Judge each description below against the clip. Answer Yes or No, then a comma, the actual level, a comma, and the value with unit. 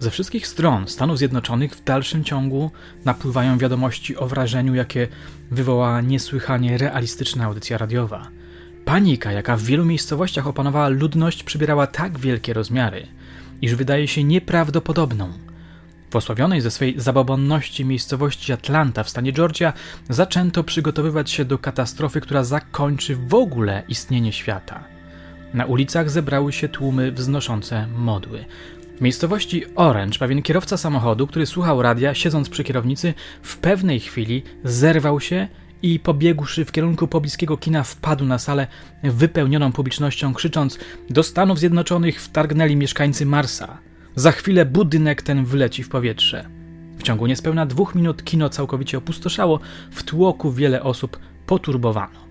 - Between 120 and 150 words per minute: Yes, average, 130 wpm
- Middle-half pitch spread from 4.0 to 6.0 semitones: Yes, average, 4.5 semitones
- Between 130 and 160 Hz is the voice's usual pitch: Yes, medium, 140 Hz